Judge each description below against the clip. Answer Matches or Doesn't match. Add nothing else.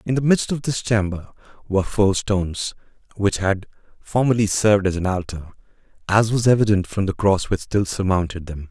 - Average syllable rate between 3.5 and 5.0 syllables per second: Doesn't match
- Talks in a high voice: Doesn't match